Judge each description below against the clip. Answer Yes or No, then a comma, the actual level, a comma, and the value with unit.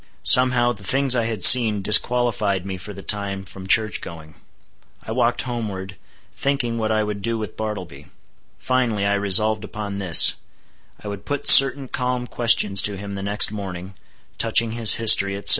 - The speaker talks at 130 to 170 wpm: Yes, average, 165 wpm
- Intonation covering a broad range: No, average, 3.1 semitones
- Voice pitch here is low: Yes, low, 105 Hz